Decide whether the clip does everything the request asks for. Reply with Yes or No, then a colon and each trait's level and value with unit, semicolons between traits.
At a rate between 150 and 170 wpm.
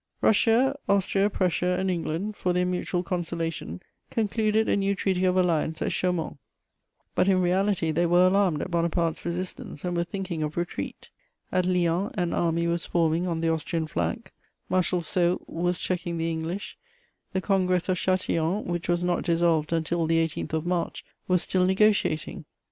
Yes: average, 165 wpm